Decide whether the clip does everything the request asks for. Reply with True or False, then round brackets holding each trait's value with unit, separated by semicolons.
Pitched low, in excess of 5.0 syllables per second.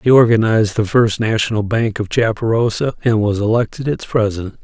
True (110 Hz; 5.5 syllables/s)